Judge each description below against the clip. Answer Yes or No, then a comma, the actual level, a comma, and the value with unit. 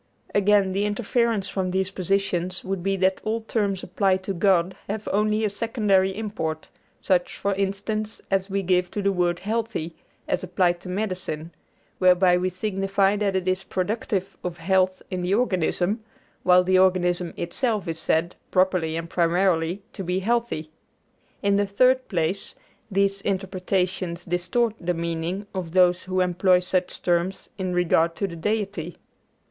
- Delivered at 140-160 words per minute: Yes, average, 155 wpm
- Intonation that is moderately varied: No, narrow, 2.1 semitones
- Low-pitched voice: No, high, 190 Hz